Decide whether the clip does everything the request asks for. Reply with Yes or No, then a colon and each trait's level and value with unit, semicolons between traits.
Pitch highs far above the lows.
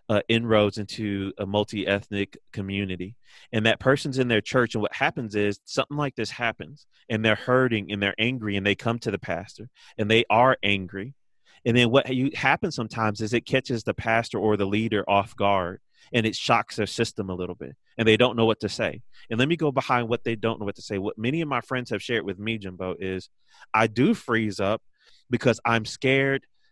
No: average, 3.3 semitones